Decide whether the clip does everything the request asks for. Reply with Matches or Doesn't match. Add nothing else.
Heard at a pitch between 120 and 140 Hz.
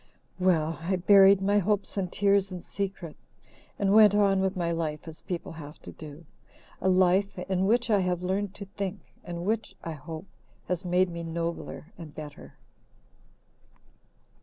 Doesn't match